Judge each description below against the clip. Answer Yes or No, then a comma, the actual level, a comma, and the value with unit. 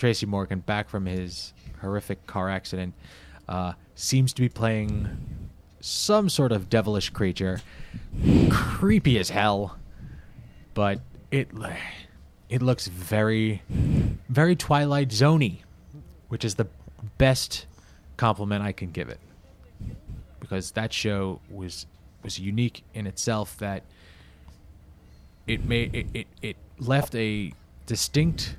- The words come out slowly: Yes, slow, 115 wpm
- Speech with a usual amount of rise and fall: Yes, average, 4.5 semitones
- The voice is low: Yes, low, 100 Hz